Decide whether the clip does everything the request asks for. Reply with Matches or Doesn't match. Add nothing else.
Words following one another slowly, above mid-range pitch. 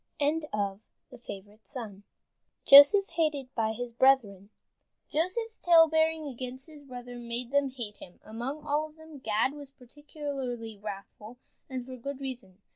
Matches